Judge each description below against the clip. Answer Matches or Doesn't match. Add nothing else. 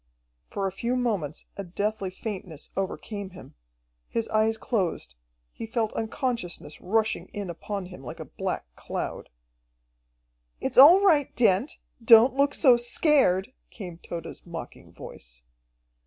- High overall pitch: Matches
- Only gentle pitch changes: Doesn't match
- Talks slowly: Matches